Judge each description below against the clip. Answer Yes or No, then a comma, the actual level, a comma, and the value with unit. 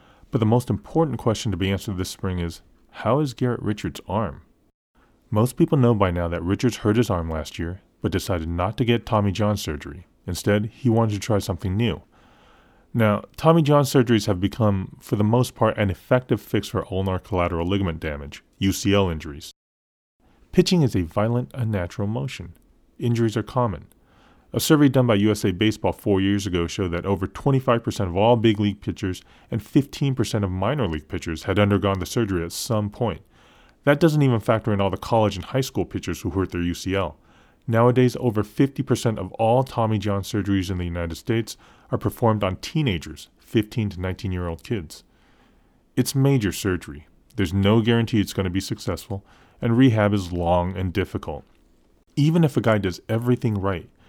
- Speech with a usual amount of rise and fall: Yes, average, 4.2 semitones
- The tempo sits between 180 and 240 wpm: Yes, average, 185 wpm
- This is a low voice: Yes, low, 105 Hz